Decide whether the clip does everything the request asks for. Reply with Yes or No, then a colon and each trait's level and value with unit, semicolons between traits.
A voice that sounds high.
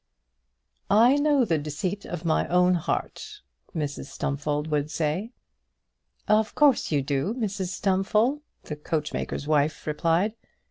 No: medium, 175 Hz